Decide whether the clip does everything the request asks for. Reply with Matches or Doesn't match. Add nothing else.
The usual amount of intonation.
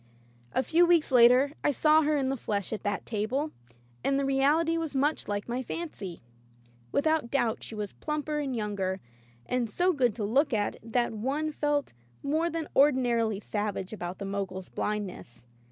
Doesn't match